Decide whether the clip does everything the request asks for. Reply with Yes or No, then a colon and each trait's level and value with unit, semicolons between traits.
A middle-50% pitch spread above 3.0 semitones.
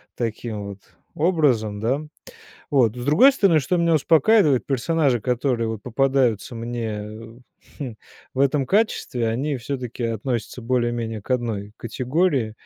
Yes: average, 4.0 semitones